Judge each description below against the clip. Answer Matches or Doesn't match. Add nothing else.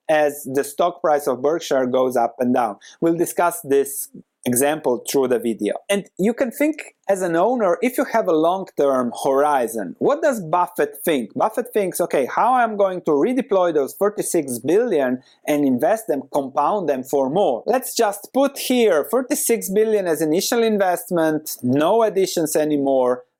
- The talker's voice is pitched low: Doesn't match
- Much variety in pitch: Matches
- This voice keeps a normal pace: Matches